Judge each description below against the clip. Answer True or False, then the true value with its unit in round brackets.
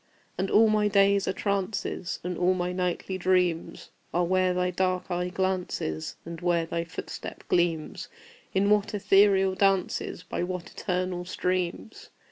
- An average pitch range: False (1.6 semitones)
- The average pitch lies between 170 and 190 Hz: True (185 Hz)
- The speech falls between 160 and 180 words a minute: False (145 wpm)